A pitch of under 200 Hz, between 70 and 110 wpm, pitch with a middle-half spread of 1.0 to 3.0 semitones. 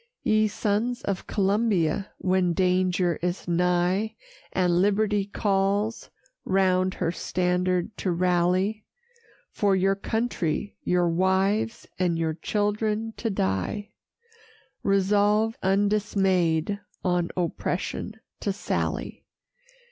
Yes: high, 190 Hz; slow, 95 wpm; narrow, 2.5 semitones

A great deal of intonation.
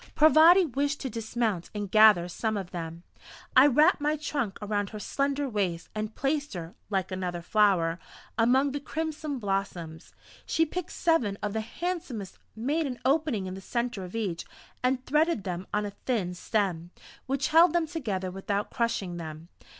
Yes: wide, 7.2 semitones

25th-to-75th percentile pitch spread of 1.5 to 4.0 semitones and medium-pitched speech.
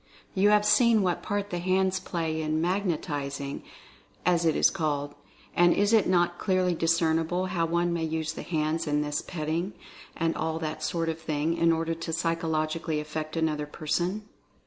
Yes: narrow, 2.4 semitones; medium, 165 Hz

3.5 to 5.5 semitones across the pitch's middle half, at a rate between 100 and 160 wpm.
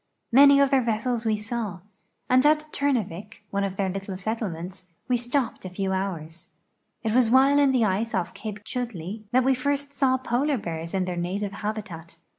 No: average, 5.2 semitones; average, 185 wpm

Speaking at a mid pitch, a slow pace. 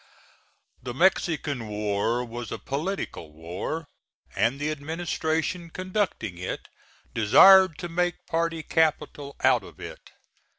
Yes: medium, 150 Hz; slow, 115 wpm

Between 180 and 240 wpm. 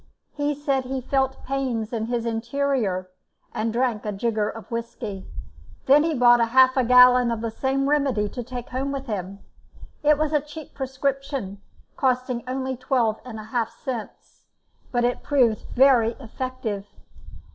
No: average, 155 wpm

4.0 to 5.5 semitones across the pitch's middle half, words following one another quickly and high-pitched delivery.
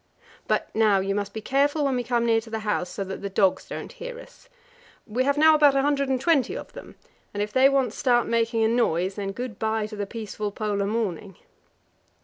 Yes: average, 4.6 semitones; fast, 225 wpm; high, 225 Hz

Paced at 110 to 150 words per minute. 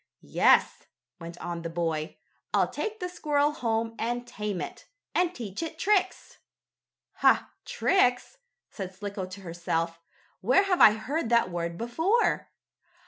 Yes: average, 140 wpm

